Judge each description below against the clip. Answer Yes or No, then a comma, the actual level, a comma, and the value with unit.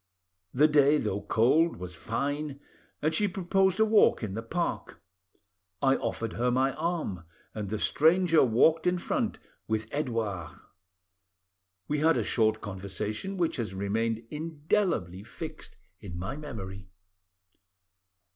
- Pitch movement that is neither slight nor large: No, wide, 7.2 semitones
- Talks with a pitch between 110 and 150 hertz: Yes, low, 135 Hz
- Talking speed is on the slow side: Yes, slow, 130 wpm